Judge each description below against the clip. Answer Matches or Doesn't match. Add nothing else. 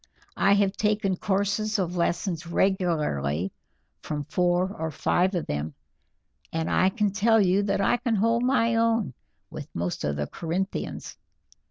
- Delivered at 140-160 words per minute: Matches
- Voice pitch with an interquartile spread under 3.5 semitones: Doesn't match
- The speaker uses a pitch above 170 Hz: Matches